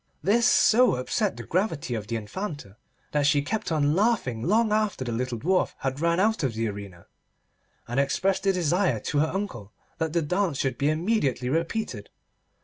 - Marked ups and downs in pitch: Yes, wide, 7.5 semitones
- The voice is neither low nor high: Yes, medium, 155 Hz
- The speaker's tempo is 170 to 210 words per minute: Yes, average, 180 wpm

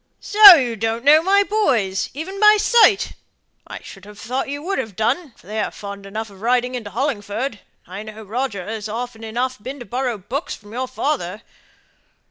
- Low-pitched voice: No, high, 240 Hz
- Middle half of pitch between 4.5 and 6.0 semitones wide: Yes, average, 5.0 semitones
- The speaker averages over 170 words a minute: Yes, average, 190 wpm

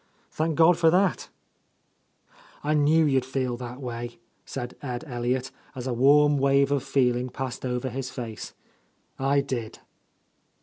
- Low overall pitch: Yes, low, 130 Hz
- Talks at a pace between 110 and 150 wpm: Yes, average, 145 wpm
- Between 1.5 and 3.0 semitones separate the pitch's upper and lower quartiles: Yes, narrow, 2.6 semitones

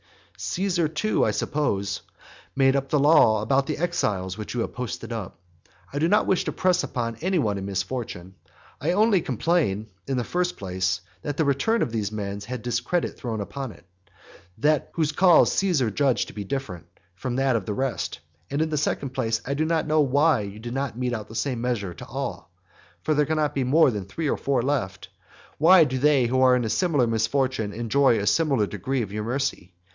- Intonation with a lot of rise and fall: Yes, wide, 5.8 semitones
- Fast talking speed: Yes, fast, 210 wpm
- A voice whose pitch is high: No, low, 130 Hz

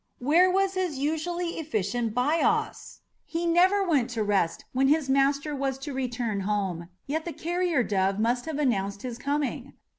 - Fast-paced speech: No, average, 160 wpm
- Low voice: No, very high, 275 Hz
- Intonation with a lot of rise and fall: Yes, wide, 5.9 semitones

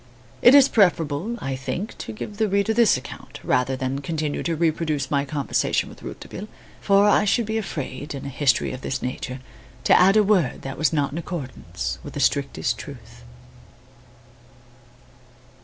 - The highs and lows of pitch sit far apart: Yes, wide, 7.0 semitones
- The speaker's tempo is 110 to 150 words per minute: No, average, 170 wpm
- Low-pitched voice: No, medium, 155 Hz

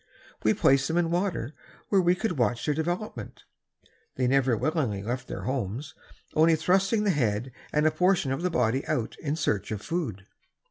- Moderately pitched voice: Yes, medium, 145 Hz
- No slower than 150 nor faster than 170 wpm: No, average, 180 wpm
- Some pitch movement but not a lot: No, wide, 6.2 semitones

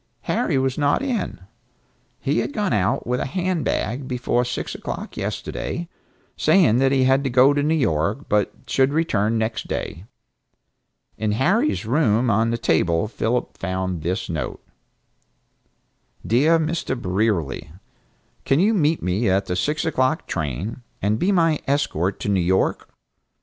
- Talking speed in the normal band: Yes, average, 150 wpm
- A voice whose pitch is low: Yes, low, 125 Hz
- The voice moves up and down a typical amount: No, wide, 6.9 semitones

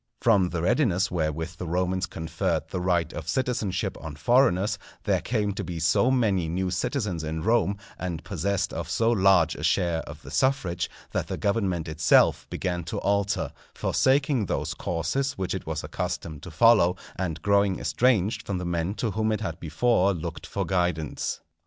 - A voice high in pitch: No, very low, 95 Hz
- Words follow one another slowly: No, average, 175 wpm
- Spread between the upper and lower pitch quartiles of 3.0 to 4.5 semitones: Yes, average, 4.0 semitones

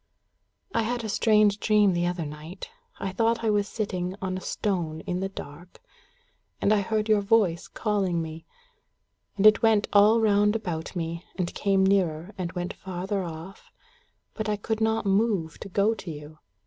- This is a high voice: Yes, high, 195 Hz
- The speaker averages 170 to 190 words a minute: Yes, average, 175 wpm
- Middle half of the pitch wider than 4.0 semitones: No, average, 3.4 semitones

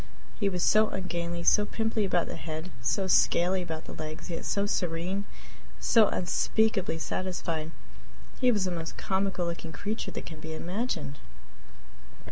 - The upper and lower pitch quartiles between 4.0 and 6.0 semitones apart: No, average, 3.4 semitones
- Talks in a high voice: No, medium, 180 Hz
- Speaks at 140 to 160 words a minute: Yes, average, 150 wpm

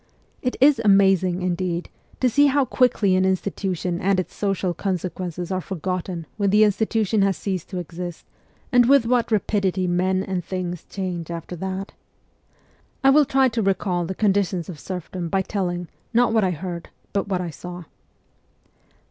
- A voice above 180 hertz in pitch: Yes, high, 190 Hz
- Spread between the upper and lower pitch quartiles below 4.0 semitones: Yes, average, 2.7 semitones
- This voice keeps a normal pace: Yes, average, 170 wpm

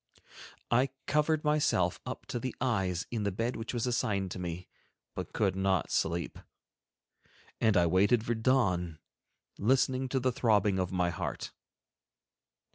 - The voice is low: Yes, low, 105 Hz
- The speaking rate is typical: Yes, average, 150 wpm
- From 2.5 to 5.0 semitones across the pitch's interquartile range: No, wide, 5.4 semitones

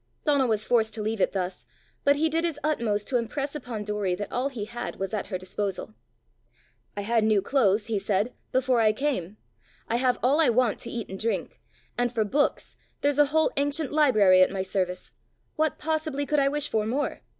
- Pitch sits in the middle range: No, high, 235 Hz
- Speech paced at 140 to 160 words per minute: No, fast, 205 wpm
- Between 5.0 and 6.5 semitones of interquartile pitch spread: Yes, wide, 5.5 semitones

